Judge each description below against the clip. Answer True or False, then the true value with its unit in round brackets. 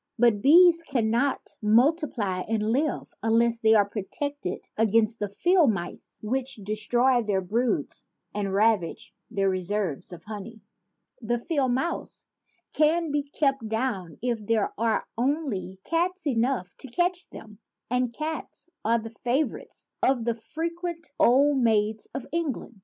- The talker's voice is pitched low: False (235 Hz)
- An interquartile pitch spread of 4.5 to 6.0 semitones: True (5.2 semitones)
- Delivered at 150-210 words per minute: False (140 wpm)